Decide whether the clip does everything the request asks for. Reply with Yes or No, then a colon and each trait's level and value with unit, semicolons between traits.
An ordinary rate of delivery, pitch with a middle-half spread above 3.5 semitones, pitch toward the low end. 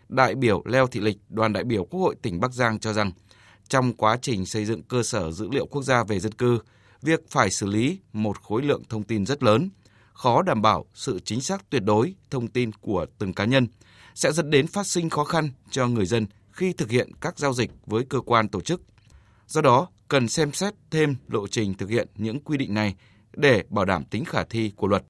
Yes: average, 230 wpm; average, 4.2 semitones; low, 115 Hz